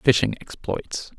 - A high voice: No, low, 115 Hz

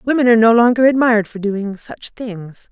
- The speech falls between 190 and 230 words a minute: Yes, average, 200 wpm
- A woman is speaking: Yes, female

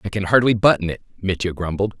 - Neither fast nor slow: No, fast, 210 wpm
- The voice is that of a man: Yes, male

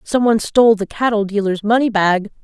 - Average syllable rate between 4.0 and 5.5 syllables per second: No, 5.8 syllables/s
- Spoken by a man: No, female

